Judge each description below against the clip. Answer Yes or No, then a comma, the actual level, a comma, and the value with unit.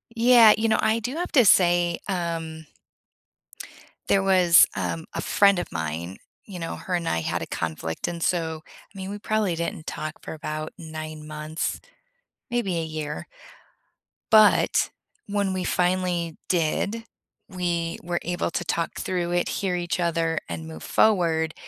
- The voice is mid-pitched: Yes, medium, 175 Hz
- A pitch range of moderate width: Yes, average, 3.3 semitones